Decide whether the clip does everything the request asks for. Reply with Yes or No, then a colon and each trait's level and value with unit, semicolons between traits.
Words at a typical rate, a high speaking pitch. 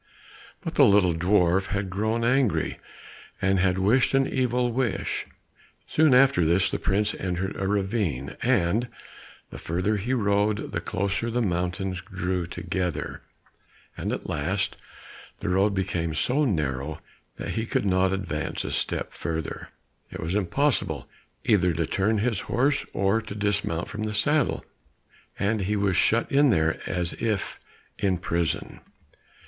No: average, 145 wpm; low, 100 Hz